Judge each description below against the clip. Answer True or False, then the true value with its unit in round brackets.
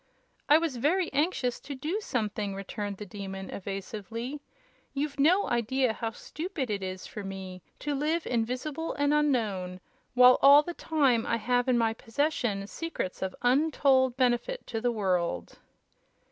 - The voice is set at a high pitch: True (245 Hz)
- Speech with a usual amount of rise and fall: False (6.0 semitones)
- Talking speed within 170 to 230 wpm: False (150 wpm)